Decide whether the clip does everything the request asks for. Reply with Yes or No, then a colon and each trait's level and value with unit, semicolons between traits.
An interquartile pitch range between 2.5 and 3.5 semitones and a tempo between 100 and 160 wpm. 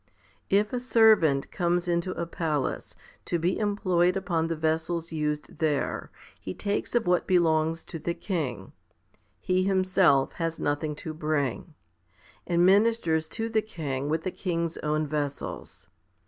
Yes: average, 3.2 semitones; average, 145 wpm